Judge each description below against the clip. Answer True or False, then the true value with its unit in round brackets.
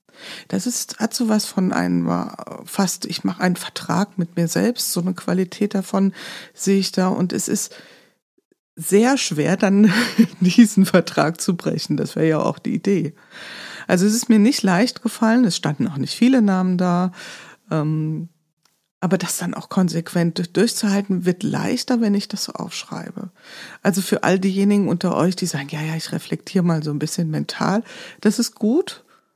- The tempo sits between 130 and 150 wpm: False (175 wpm)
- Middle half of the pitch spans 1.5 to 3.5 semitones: False (3.9 semitones)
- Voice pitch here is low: False (195 Hz)